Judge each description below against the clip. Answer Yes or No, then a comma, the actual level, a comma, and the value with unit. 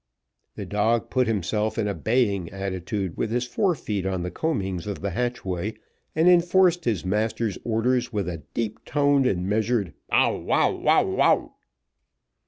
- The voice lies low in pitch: Yes, low, 110 Hz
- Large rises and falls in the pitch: No, average, 4.2 semitones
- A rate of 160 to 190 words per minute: No, average, 150 wpm